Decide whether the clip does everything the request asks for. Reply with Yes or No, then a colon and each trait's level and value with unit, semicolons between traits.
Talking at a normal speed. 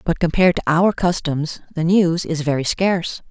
Yes: average, 180 wpm